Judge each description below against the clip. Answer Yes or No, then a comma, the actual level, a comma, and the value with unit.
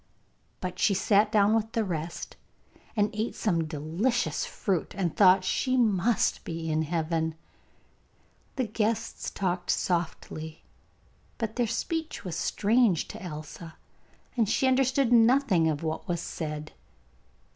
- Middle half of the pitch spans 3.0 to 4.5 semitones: No, wide, 5.6 semitones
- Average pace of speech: No, slow, 130 wpm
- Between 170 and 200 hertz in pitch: Yes, high, 190 Hz